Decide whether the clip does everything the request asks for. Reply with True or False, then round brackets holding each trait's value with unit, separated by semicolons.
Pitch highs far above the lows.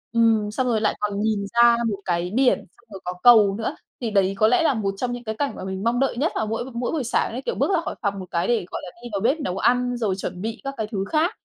False (3.6 semitones)